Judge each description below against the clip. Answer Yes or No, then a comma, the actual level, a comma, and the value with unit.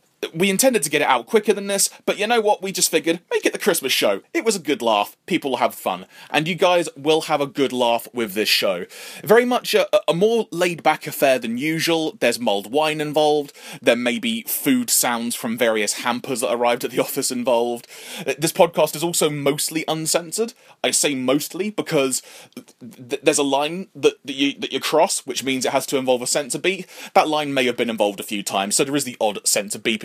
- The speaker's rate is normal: No, fast, 230 wpm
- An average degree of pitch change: No, wide, 6.2 semitones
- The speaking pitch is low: No, medium, 155 Hz